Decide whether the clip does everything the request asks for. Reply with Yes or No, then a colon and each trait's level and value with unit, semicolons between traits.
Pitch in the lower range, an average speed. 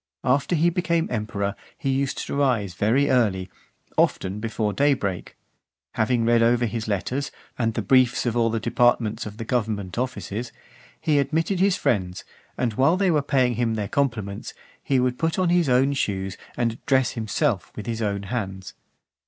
Yes: low, 120 Hz; average, 170 wpm